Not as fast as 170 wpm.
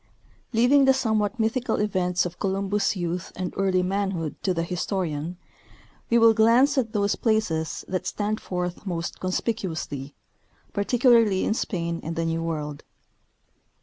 Yes: average, 140 wpm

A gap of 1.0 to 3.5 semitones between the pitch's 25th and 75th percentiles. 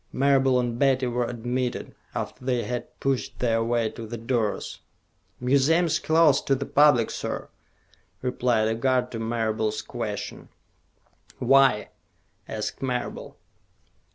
Yes: average, 2.7 semitones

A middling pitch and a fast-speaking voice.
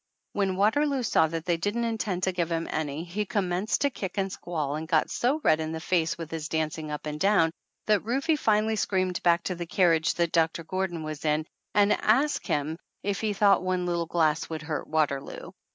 Yes: medium, 175 Hz; fast, 215 wpm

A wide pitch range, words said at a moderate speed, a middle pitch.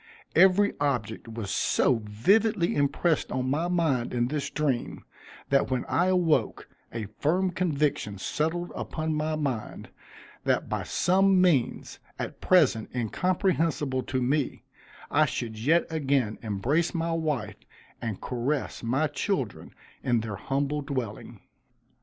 No: wide, 5.8 semitones; slow, 130 wpm; medium, 145 Hz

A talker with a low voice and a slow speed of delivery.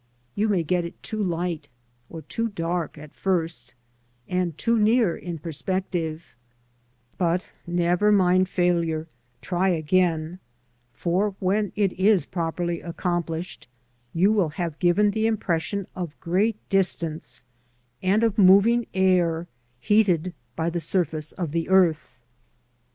No: medium, 180 Hz; slow, 125 wpm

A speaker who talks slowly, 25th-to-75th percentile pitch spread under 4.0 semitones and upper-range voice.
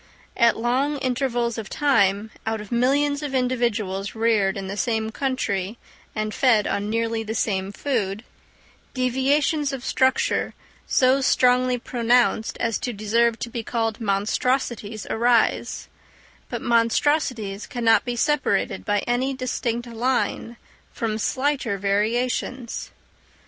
Yes: slow, 125 wpm; average, 3.0 semitones; high, 235 Hz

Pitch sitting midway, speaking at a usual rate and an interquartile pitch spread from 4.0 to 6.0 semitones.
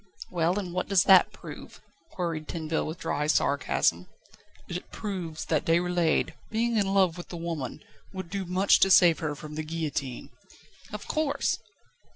No: medium, 170 Hz; average, 160 wpm; average, 3.3 semitones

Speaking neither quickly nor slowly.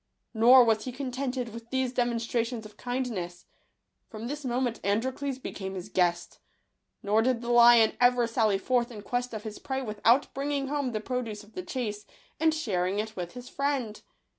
Yes: average, 175 wpm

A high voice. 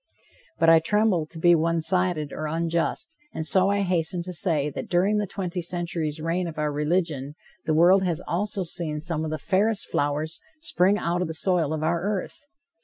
No: medium, 170 Hz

